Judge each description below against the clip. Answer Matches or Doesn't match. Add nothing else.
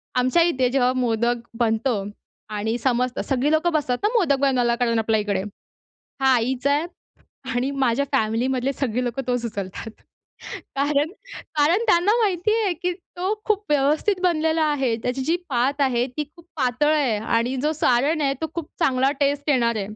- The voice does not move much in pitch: Doesn't match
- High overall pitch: Matches